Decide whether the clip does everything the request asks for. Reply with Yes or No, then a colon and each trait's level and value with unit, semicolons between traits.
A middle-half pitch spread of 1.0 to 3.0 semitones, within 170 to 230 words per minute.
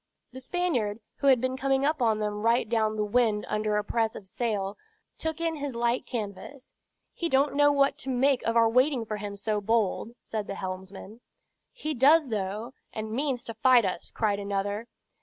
No: average, 4.2 semitones; average, 190 wpm